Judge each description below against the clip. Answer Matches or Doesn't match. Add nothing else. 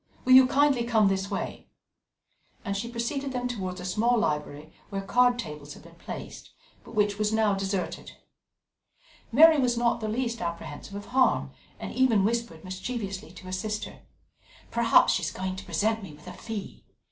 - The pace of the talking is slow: Doesn't match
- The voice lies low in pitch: Doesn't match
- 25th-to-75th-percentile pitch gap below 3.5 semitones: Doesn't match